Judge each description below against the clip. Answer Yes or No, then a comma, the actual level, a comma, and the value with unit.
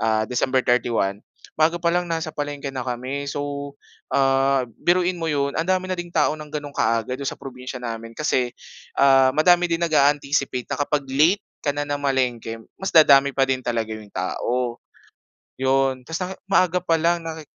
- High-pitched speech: No, medium, 140 Hz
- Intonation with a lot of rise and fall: No, average, 4.1 semitones